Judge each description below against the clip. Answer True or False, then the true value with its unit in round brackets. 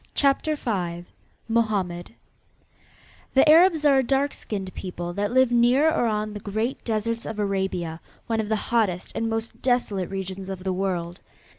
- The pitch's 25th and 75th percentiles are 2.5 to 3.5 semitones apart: False (4.3 semitones)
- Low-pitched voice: False (215 Hz)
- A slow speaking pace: False (160 wpm)